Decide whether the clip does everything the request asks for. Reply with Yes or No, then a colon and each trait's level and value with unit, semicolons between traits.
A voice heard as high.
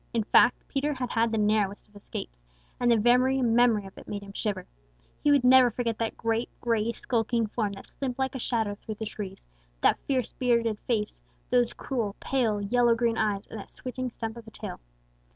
Yes: high, 230 Hz